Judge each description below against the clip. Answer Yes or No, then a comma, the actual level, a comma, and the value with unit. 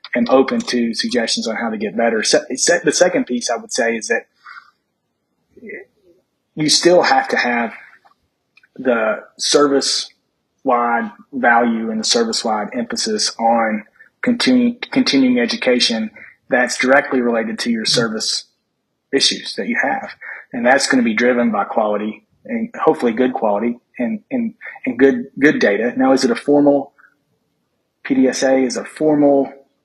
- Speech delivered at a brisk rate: No, average, 140 wpm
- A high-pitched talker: No, medium, 140 Hz